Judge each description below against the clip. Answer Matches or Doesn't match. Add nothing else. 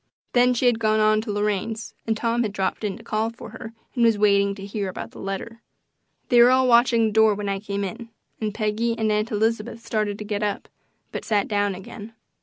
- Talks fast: Matches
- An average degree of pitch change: Doesn't match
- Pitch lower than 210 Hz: Doesn't match